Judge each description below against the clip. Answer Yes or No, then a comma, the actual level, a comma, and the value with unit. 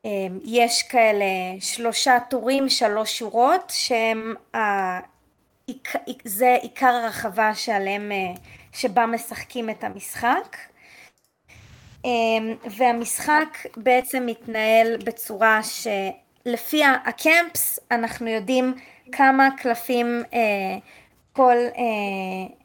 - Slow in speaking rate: Yes, slow, 70 wpm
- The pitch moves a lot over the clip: No, narrow, 2.4 semitones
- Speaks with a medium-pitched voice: No, high, 235 Hz